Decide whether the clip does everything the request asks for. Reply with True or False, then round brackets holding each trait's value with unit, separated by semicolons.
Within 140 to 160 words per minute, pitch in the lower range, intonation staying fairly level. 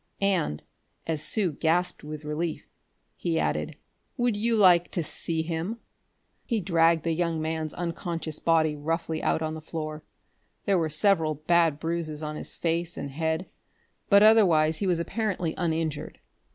False (150 wpm; 165 Hz; 2.1 semitones)